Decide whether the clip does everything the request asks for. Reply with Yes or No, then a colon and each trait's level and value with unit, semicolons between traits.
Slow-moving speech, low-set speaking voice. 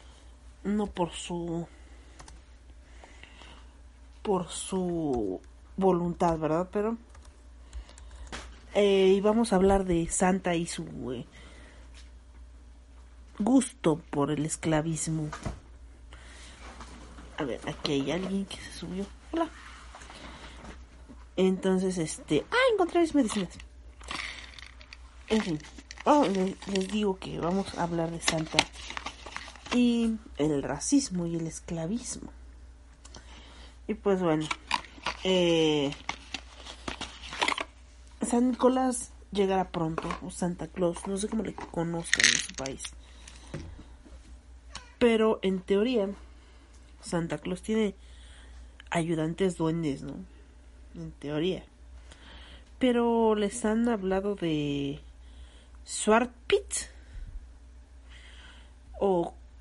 No: slow, 95 wpm; medium, 155 Hz